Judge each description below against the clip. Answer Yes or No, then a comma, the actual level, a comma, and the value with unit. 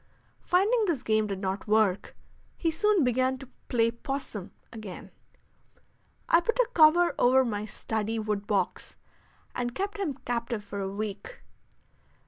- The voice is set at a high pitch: Yes, high, 240 Hz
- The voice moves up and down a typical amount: No, wide, 7.6 semitones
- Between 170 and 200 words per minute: No, average, 140 wpm